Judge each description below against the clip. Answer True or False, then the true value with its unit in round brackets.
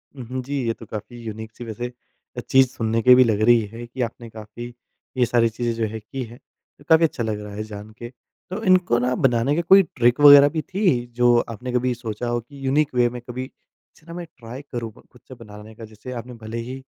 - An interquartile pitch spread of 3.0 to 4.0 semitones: False (2.5 semitones)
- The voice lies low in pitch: True (120 Hz)